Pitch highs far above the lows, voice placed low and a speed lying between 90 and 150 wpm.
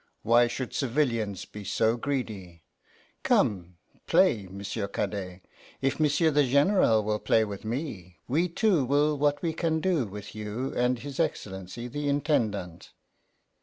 Yes: wide, 6.2 semitones; low, 120 Hz; average, 140 wpm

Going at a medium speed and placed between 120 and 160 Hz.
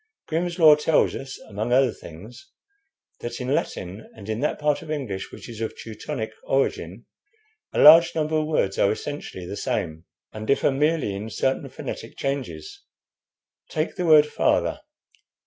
Yes: average, 160 wpm; low, 135 Hz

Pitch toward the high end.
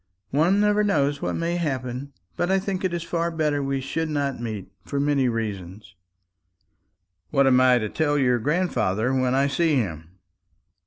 No: medium, 140 Hz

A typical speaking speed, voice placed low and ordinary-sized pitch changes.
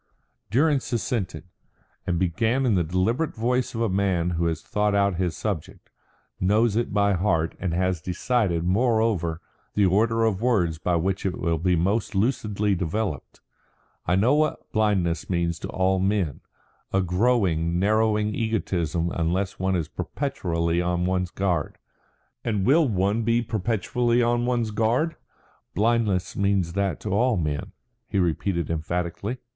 Yes: average, 150 wpm; very low, 95 Hz; average, 4.4 semitones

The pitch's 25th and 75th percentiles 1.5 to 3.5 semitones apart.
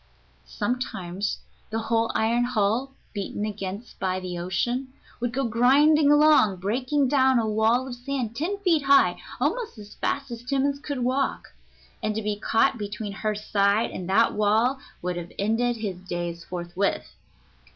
No: average, 4.5 semitones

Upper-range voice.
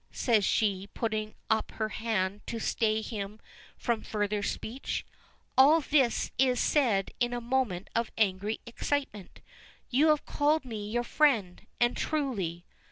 Yes: high, 225 Hz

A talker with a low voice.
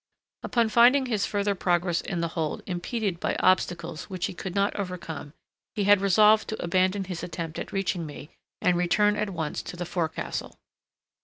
No: medium, 185 Hz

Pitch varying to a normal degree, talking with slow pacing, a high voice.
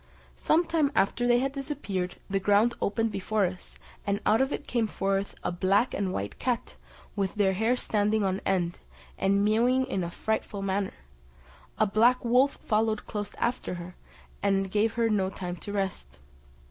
No: average, 3.4 semitones; average, 170 wpm; high, 205 Hz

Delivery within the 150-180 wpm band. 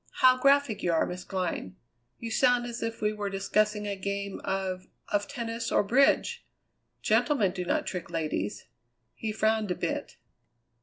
Yes: average, 160 wpm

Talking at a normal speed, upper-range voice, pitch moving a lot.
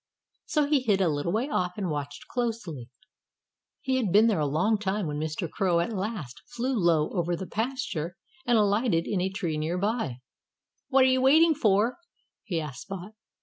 Yes: average, 190 wpm; high, 195 Hz; wide, 6.0 semitones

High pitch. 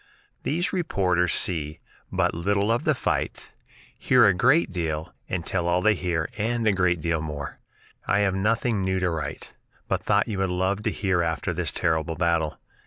No: very low, 90 Hz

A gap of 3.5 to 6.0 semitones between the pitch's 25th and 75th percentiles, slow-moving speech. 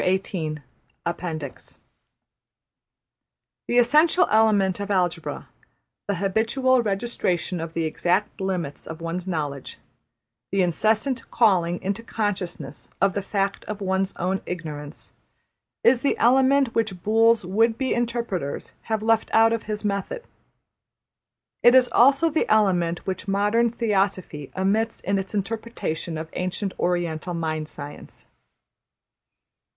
Yes: average, 4.6 semitones; slow, 120 wpm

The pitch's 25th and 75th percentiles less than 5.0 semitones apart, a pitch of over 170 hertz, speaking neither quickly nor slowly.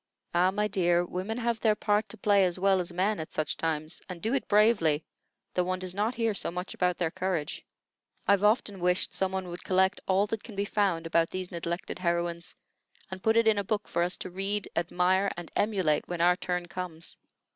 No: average, 2.8 semitones; medium, 185 Hz; fast, 215 wpm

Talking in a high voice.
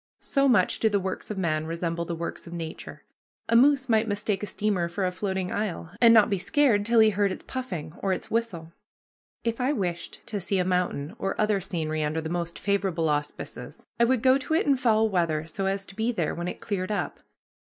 Yes: high, 195 Hz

